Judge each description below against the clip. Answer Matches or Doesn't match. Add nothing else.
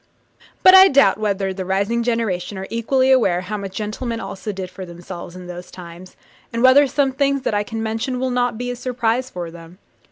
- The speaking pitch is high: Matches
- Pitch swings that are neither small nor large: Matches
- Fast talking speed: Matches